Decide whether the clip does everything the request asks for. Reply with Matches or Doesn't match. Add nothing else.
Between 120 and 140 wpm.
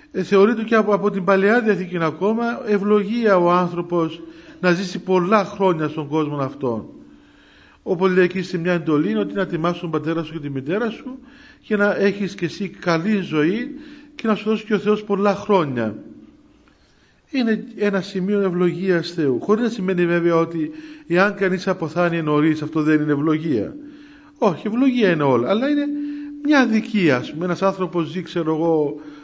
Doesn't match